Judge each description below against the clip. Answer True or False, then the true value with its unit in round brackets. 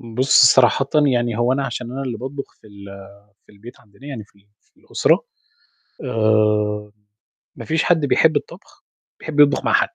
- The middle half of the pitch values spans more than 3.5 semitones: True (4.3 semitones)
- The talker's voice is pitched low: True (120 Hz)